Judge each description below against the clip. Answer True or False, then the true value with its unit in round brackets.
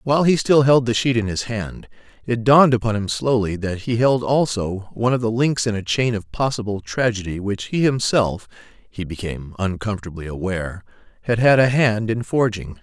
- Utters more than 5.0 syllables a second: True (5.3 syllables/s)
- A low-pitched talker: True (110 Hz)